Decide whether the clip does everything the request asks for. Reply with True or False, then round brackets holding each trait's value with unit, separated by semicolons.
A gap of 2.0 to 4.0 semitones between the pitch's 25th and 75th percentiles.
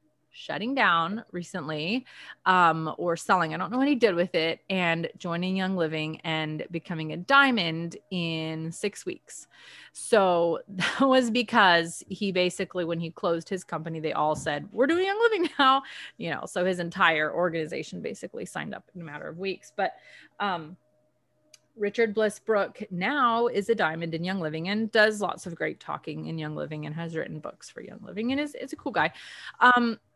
False (5.5 semitones)